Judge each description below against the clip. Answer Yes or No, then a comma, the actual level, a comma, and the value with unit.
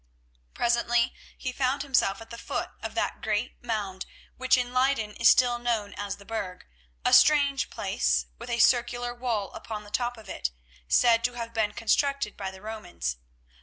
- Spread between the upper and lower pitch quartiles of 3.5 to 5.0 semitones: No, average, 2.8 semitones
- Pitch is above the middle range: Yes, high, 235 Hz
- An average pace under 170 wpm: No, average, 175 wpm